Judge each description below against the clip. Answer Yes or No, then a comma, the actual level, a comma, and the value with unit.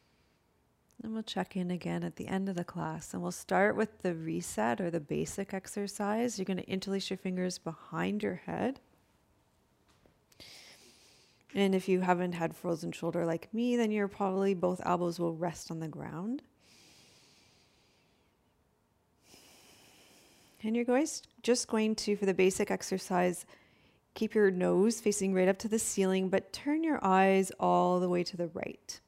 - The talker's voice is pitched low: No, high, 190 Hz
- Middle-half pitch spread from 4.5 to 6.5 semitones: No, average, 2.8 semitones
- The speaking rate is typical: Yes, average, 165 wpm